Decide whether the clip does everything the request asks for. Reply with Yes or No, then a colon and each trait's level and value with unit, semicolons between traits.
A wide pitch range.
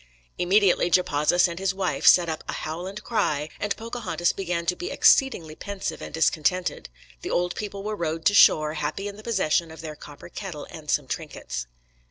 No: average, 4.1 semitones